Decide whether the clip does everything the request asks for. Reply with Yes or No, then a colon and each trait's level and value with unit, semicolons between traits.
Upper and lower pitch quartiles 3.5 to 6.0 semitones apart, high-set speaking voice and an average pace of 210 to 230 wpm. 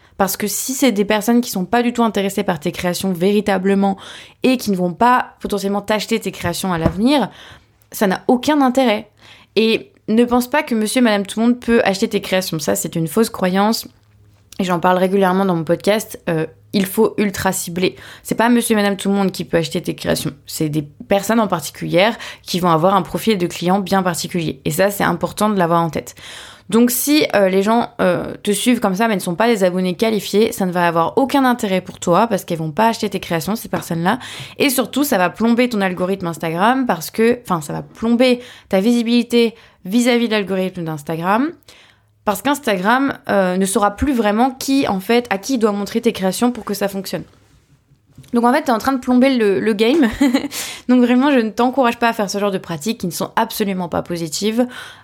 Yes: average, 4.5 semitones; high, 205 Hz; fast, 220 wpm